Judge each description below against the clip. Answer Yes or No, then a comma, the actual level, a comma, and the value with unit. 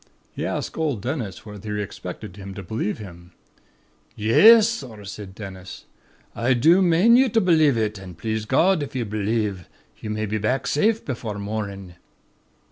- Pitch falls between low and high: No, low, 110 Hz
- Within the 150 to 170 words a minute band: Yes, average, 165 wpm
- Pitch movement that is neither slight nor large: No, wide, 6.5 semitones